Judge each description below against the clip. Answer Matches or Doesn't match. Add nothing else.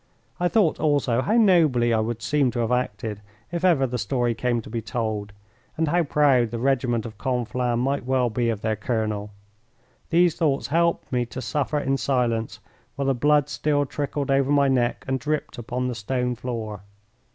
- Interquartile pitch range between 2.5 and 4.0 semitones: Matches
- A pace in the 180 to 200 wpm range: Matches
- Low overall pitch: Matches